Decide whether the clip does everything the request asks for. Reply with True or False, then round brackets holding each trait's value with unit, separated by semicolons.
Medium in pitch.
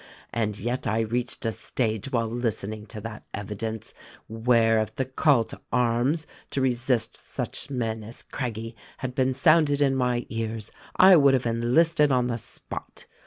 False (120 Hz)